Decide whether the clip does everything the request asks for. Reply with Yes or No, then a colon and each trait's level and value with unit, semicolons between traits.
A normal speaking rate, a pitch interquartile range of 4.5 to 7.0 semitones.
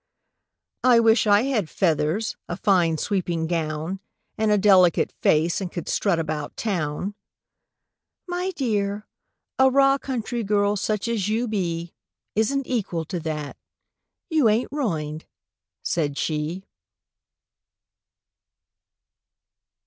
No: slow, 110 wpm; wide, 5.4 semitones